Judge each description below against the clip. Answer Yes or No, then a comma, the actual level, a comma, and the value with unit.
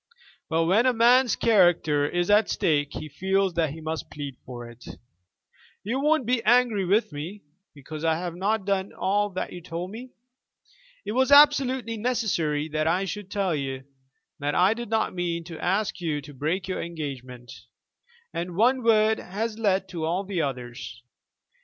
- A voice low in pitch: No, medium, 185 Hz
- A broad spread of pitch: Yes, wide, 5.8 semitones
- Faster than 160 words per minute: Yes, average, 170 wpm